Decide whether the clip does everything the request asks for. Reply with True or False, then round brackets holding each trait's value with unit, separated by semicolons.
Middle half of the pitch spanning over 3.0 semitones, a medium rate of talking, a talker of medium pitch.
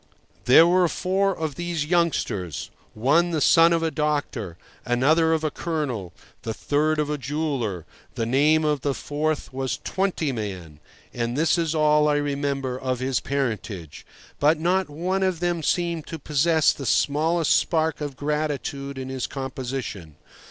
True (3.7 semitones; 155 wpm; 150 Hz)